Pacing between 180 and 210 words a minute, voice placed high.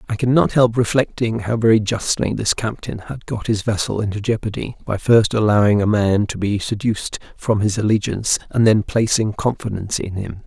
No: average, 190 wpm; low, 110 Hz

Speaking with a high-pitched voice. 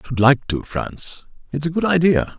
No: medium, 145 Hz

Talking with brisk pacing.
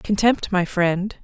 No: average, 145 wpm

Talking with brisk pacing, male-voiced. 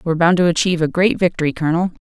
No: fast, 235 wpm; female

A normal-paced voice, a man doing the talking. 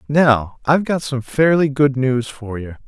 Yes: average, 190 wpm; male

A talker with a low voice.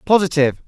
No: medium, 160 Hz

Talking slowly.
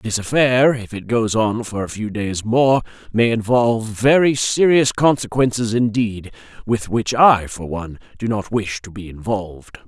No: average, 170 wpm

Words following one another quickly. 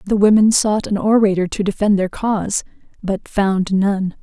No: average, 170 wpm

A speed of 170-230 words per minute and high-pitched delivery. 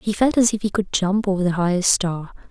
No: fast, 265 wpm; high, 195 Hz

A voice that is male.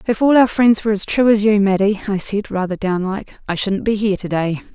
No: female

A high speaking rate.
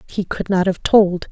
Yes: fast, 230 wpm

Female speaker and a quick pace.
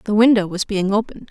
Yes: female; fast, 230 wpm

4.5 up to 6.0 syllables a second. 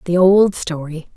No: 4.0 syllables/s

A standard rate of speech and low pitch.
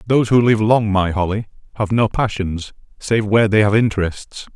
Yes: average, 185 wpm; low, 105 Hz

